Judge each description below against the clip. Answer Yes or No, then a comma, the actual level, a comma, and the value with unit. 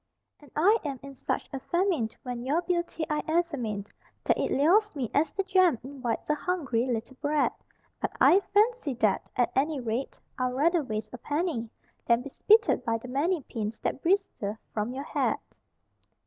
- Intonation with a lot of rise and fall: Yes, wide, 5.9 semitones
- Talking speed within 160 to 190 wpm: Yes, average, 175 wpm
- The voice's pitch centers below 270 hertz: No, very high, 280 Hz